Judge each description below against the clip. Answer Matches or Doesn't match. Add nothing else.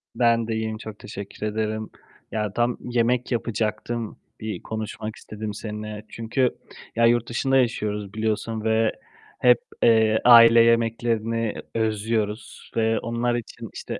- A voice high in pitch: Doesn't match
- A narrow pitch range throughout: Matches